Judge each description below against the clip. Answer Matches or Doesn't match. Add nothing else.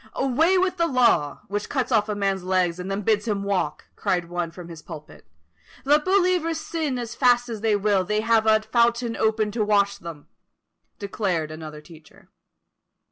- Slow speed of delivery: Doesn't match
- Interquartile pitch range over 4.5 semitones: Matches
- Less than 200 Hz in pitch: Doesn't match